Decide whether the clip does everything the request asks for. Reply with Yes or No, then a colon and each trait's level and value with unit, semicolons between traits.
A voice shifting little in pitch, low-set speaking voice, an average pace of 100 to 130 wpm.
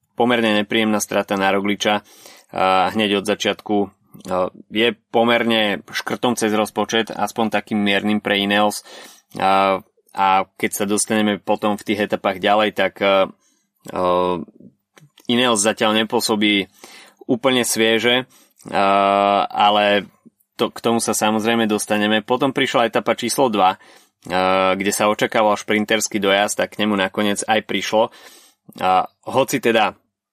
Yes: narrow, 2.1 semitones; low, 105 Hz; average, 115 wpm